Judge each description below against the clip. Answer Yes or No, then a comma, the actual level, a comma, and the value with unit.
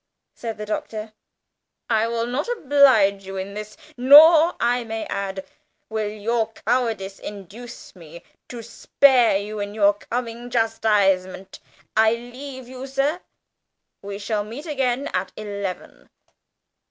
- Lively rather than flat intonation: No, average, 3.4 semitones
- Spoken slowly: Yes, slow, 130 wpm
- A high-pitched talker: Yes, high, 225 Hz